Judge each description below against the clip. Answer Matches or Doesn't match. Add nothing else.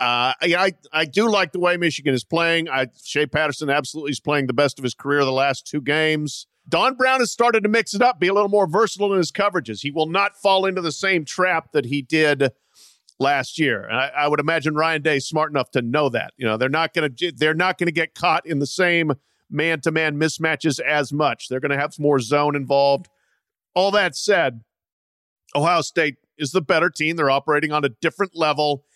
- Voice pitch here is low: Doesn't match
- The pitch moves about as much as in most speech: Matches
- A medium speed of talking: Doesn't match